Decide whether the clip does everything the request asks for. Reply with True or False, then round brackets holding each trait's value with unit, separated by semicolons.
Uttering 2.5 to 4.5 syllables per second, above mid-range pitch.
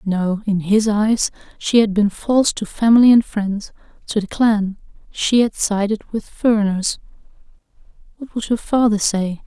True (4.4 syllables/s; 210 Hz)